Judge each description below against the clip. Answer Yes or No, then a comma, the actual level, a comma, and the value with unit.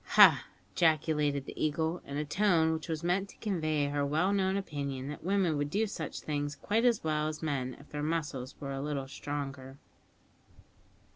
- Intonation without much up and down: No, average, 3.0 semitones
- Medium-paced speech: Yes, average, 185 wpm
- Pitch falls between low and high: Yes, medium, 150 Hz